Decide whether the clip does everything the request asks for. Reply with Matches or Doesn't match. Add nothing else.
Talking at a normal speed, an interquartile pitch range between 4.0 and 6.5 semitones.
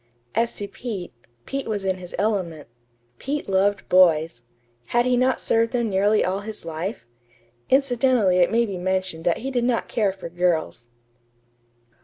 Matches